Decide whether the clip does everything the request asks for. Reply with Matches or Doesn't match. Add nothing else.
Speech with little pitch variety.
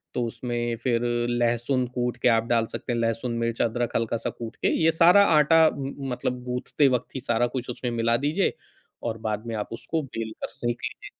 Matches